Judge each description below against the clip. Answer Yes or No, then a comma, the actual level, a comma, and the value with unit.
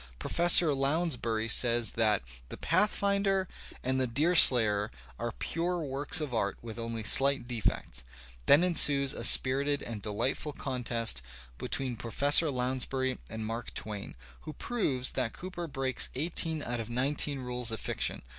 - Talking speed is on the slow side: No, average, 145 wpm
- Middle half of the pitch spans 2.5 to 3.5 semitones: No, average, 4.5 semitones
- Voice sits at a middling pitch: No, low, 130 Hz